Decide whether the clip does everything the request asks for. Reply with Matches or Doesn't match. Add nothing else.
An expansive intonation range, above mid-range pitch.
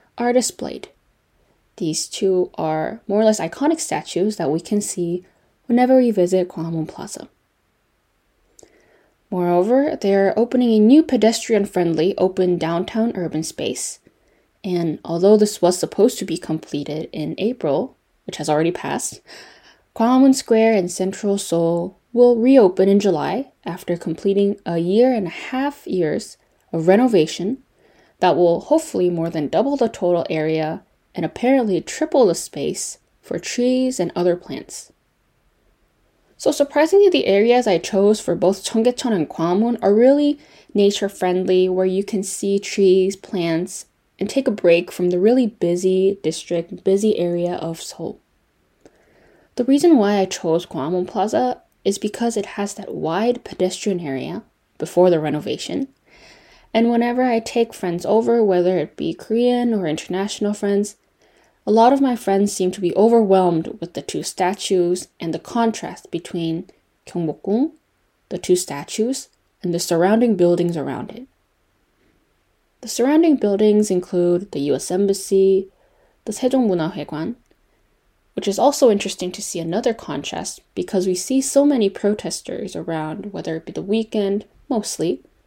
Doesn't match